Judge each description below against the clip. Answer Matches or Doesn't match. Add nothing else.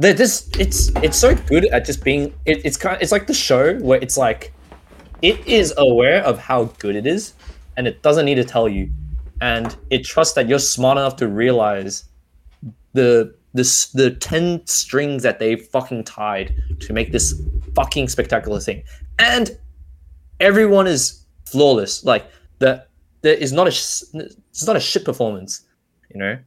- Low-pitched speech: Matches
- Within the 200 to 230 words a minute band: Doesn't match